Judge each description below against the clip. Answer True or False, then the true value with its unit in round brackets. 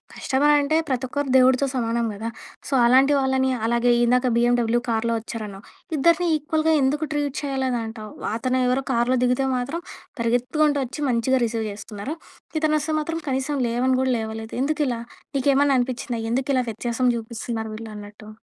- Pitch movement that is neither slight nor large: True (3.1 semitones)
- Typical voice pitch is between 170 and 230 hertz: False (255 Hz)